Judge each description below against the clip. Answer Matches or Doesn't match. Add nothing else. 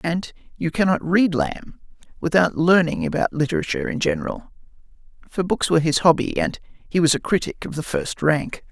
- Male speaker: Matches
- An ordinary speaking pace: Matches